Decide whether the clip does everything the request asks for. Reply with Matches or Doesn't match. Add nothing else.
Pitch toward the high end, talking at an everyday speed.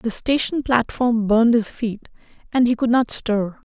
Matches